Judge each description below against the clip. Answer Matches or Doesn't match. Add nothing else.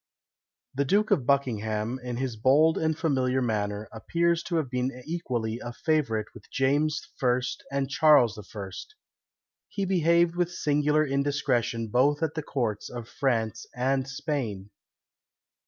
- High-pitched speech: Doesn't match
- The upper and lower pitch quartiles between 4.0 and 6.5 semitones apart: Matches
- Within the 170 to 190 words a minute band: Doesn't match